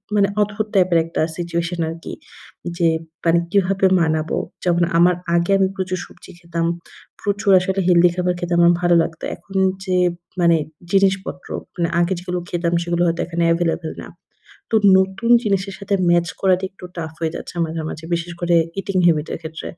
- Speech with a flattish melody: Yes, narrow, 2.1 semitones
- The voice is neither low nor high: Yes, medium, 175 Hz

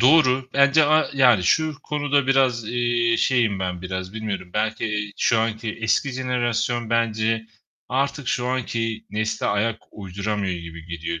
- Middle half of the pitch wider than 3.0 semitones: Yes, average, 3.7 semitones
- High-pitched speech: No, low, 115 Hz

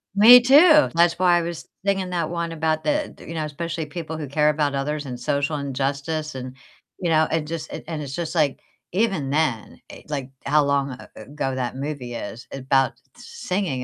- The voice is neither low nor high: Yes, medium, 155 Hz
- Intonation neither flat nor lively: Yes, average, 3.6 semitones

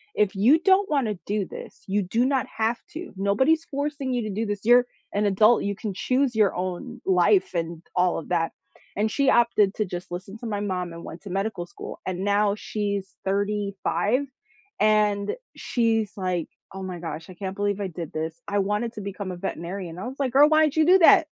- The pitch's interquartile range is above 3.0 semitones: Yes, average, 4.0 semitones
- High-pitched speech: Yes, high, 205 Hz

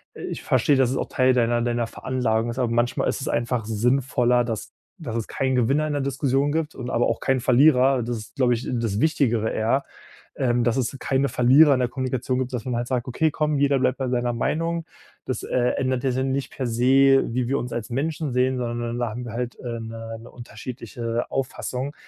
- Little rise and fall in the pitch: Yes, narrow, 2.2 semitones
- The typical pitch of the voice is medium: No, low, 125 Hz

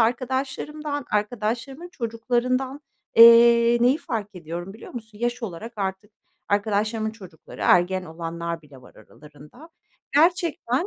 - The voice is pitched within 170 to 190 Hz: No, high, 225 Hz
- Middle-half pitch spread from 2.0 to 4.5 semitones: No, average, 5.0 semitones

